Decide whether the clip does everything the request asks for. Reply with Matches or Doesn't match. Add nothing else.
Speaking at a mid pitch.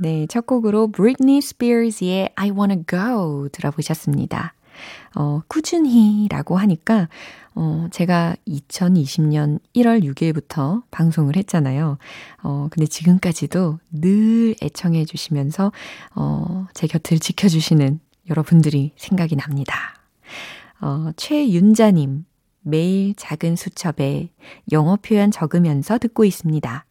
Matches